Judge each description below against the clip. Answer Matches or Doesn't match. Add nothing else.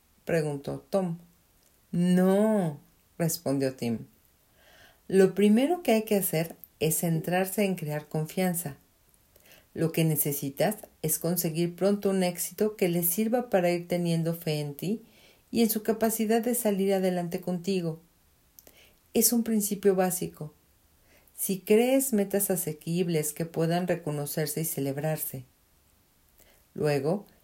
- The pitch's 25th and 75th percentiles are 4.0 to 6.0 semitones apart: Matches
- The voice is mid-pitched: Matches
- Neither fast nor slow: Doesn't match